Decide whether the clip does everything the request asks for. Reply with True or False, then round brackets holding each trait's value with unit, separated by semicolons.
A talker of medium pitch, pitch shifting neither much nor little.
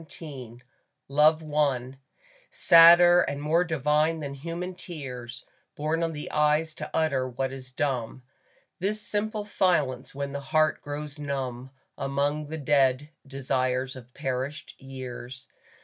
True (145 Hz; 3.3 semitones)